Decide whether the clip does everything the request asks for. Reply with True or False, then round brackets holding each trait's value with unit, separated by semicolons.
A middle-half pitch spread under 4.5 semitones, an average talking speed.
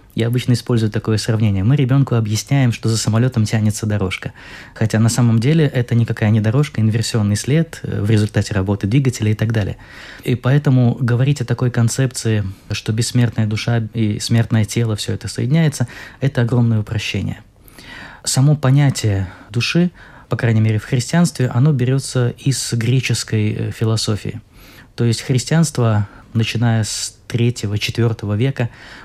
True (2.7 semitones; 140 wpm)